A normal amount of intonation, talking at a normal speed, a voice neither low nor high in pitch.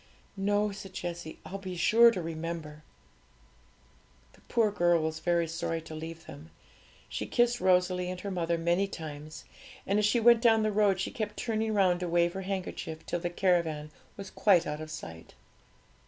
Yes: average, 3.5 semitones; average, 180 wpm; medium, 180 Hz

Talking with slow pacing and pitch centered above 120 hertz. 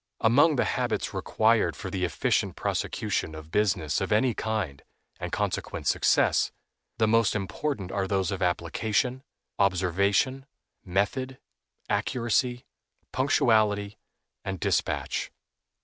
No: slow, 110 wpm; low, 105 Hz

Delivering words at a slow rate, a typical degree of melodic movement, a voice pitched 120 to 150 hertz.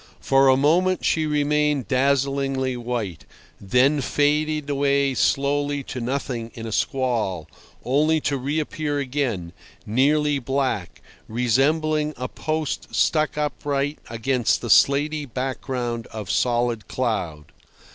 Yes: slow, 115 wpm; average, 3.3 semitones; low, 135 Hz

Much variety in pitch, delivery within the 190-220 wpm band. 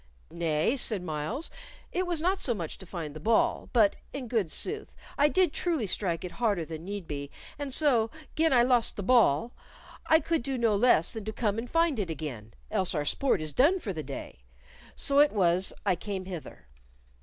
Yes: wide, 8.1 semitones; average, 200 wpm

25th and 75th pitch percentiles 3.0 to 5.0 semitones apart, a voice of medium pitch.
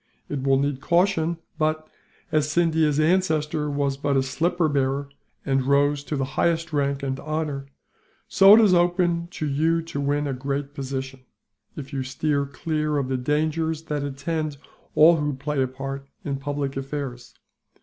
No: narrow, 2.5 semitones; medium, 145 Hz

